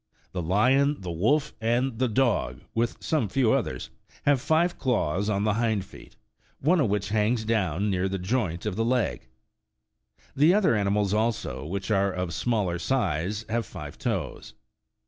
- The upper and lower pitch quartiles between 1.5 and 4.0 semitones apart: No, average, 4.6 semitones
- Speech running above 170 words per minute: No, average, 165 wpm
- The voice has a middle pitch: No, low, 110 Hz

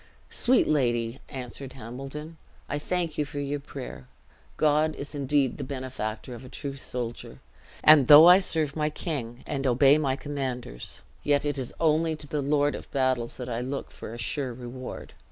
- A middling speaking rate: Yes, average, 175 wpm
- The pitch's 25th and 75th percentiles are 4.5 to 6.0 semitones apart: No, average, 3.0 semitones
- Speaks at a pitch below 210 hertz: Yes, medium, 140 Hz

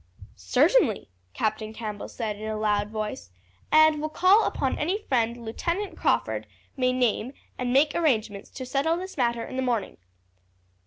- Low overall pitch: No, high, 245 Hz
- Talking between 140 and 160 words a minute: Yes, average, 155 wpm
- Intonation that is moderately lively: No, wide, 6.0 semitones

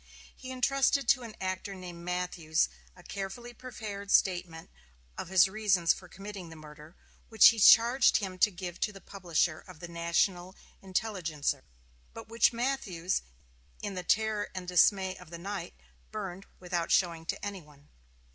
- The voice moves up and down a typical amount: Yes, average, 3.4 semitones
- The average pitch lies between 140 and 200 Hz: Yes, medium, 185 Hz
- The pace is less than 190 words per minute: Yes, average, 155 wpm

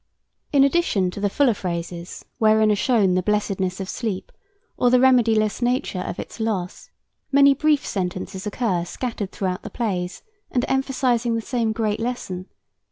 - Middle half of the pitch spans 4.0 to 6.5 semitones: Yes, average, 4.8 semitones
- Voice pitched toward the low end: No, high, 215 Hz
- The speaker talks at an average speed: Yes, average, 160 wpm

